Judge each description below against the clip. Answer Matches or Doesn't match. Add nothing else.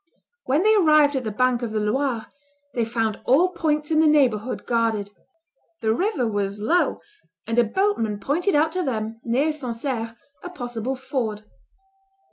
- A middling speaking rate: Matches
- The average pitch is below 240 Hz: Doesn't match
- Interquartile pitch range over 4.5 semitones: Matches